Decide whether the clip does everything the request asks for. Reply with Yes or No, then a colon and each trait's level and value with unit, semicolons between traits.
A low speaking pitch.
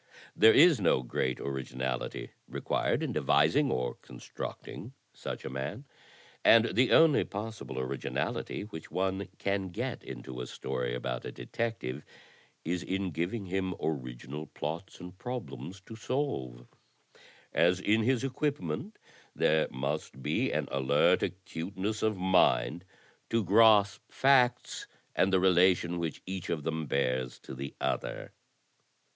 Yes: very low, 90 Hz